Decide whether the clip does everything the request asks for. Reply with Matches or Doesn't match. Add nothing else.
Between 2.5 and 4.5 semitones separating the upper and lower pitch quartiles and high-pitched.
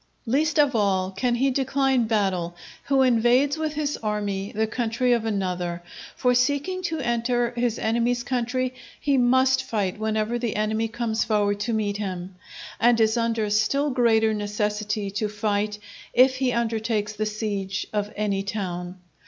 Matches